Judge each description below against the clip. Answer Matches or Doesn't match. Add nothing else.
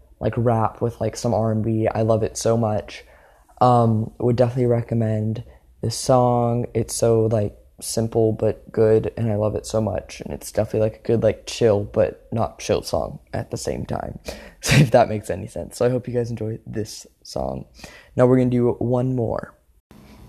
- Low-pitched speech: Matches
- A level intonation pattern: Matches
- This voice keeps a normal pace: Matches